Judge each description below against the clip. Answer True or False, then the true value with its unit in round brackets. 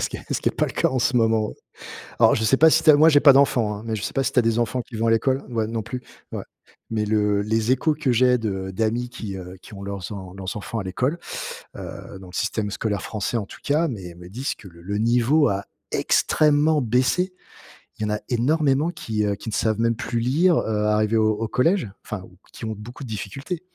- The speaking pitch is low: True (115 Hz)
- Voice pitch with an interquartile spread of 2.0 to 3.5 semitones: False (4.1 semitones)